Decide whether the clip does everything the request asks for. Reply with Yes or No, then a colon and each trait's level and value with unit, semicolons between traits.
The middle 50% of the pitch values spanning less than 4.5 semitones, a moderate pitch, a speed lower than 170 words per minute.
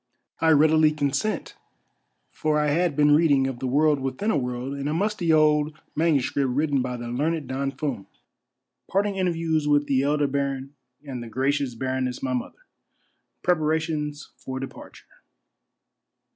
Yes: average, 2.8 semitones; medium, 145 Hz; average, 160 wpm